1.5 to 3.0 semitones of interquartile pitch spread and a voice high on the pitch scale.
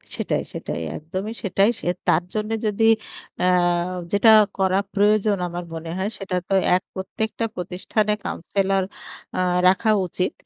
Yes: narrow, 2.6 semitones; high, 195 Hz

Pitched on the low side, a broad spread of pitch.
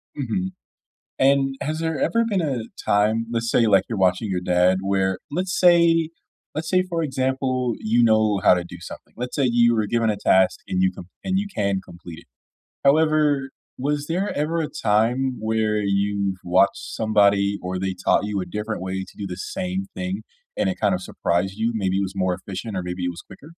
Yes: low, 110 Hz; wide, 7.1 semitones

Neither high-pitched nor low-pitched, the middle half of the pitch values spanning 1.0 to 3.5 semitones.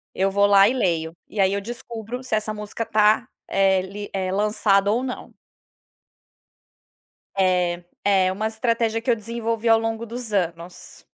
No: high, 210 Hz; average, 2.8 semitones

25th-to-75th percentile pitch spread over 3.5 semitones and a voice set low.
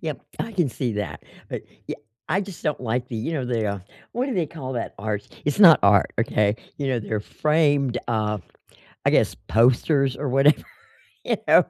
Yes: wide, 5.6 semitones; low, 130 Hz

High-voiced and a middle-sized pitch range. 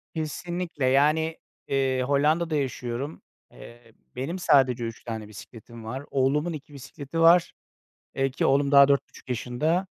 No: medium, 140 Hz; average, 3.7 semitones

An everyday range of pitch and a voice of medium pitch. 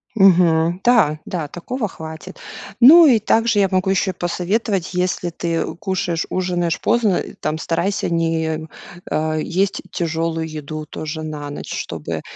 Yes: average, 3.3 semitones; medium, 170 Hz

